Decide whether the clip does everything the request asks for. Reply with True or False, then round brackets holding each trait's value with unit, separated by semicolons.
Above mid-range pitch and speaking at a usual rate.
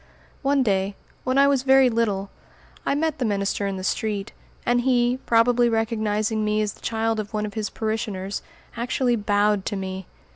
True (220 Hz; 180 wpm)